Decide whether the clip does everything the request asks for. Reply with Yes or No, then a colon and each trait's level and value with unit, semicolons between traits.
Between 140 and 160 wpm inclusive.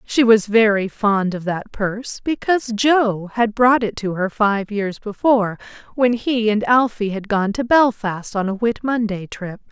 No: average, 185 wpm